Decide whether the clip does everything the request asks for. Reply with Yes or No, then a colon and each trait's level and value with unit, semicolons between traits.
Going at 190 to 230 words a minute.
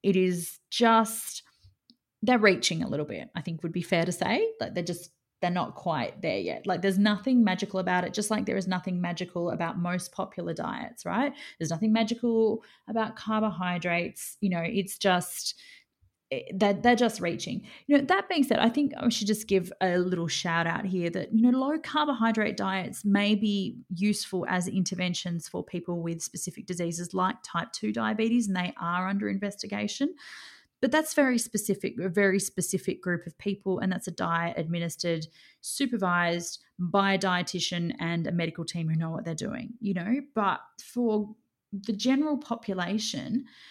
No: average, 175 wpm